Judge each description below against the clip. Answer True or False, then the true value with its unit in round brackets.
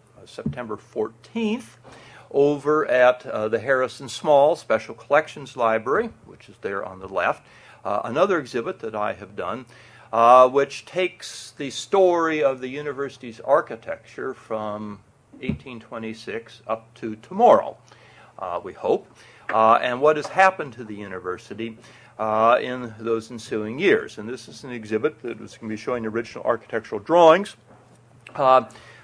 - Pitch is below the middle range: True (120 Hz)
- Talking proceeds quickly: False (145 wpm)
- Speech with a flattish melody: False (3.7 semitones)